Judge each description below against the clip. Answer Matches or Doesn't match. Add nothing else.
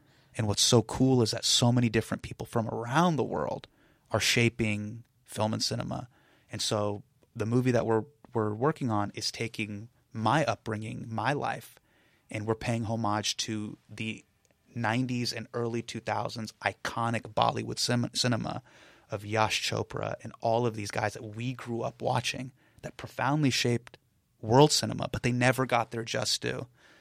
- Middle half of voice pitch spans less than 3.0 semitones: Matches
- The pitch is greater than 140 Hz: Doesn't match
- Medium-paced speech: Matches